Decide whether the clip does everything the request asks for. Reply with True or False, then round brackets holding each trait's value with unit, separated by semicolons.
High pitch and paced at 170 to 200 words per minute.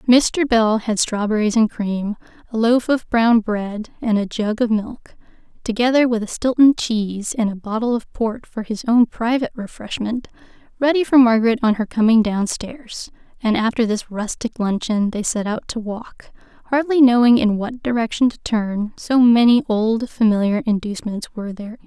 True (225 Hz; 180 wpm)